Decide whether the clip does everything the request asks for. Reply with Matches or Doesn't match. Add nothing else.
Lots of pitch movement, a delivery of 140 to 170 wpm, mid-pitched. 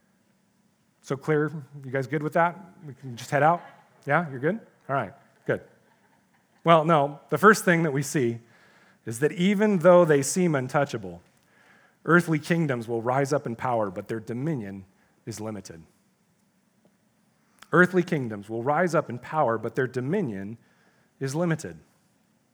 Matches